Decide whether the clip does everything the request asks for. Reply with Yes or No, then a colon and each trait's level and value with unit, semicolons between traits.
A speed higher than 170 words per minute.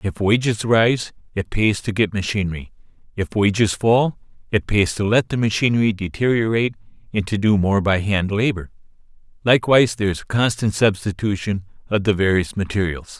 No: average, 155 wpm